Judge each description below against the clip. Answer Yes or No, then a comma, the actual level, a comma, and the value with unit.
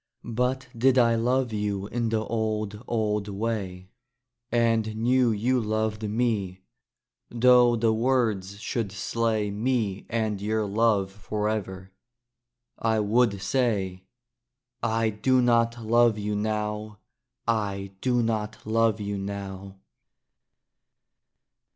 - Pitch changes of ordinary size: No, narrow, 2.3 semitones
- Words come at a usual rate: No, slow, 110 wpm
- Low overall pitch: Yes, low, 110 Hz